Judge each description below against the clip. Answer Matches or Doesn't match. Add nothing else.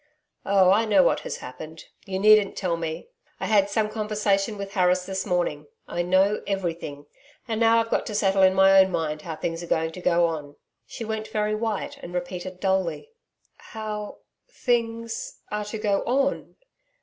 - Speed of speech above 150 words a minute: Matches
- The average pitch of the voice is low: Doesn't match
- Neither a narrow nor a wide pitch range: Matches